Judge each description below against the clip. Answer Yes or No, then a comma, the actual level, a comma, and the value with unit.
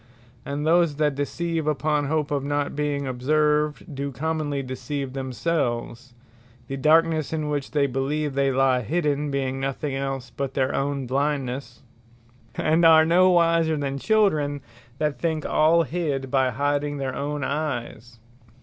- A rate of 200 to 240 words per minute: No, average, 145 wpm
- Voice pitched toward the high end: No, medium, 145 Hz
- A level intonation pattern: Yes, narrow, 2.3 semitones